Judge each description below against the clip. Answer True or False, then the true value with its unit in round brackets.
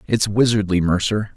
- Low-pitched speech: True (105 Hz)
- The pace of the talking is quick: False (130 wpm)